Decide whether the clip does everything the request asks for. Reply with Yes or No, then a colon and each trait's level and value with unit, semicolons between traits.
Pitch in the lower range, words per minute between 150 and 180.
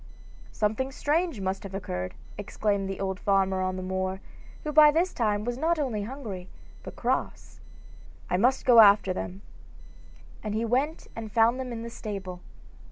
No: high, 210 Hz; average, 165 wpm